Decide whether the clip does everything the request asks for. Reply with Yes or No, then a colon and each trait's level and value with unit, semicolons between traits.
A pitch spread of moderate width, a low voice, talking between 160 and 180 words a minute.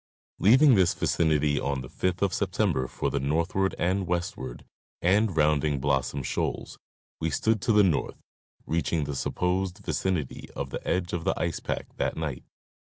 Yes: average, 4.6 semitones; very low, 85 Hz; average, 170 wpm